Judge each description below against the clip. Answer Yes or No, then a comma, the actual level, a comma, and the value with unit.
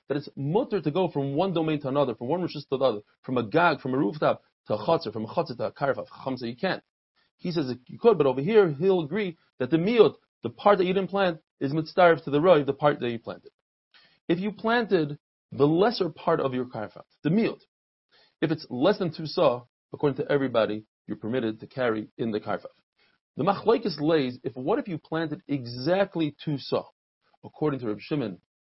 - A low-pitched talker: No, medium, 150 Hz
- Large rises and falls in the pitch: Yes, wide, 6.3 semitones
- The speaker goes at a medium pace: No, fast, 210 wpm